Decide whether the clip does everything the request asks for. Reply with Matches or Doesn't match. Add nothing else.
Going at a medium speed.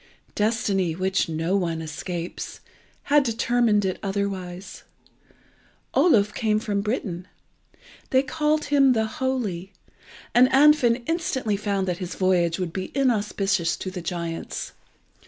Doesn't match